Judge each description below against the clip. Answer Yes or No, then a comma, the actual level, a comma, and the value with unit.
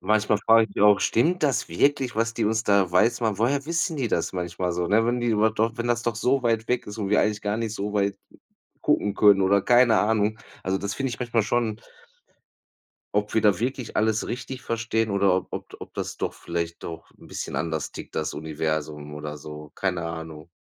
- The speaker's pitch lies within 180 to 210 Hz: No, low, 105 Hz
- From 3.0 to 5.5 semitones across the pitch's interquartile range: Yes, average, 4.4 semitones